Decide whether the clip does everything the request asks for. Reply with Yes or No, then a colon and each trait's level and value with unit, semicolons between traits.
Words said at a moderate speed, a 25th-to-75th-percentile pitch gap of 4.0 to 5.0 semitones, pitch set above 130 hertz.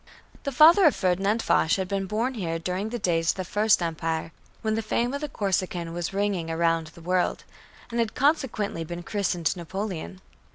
Yes: average, 190 wpm; average, 4.5 semitones; high, 190 Hz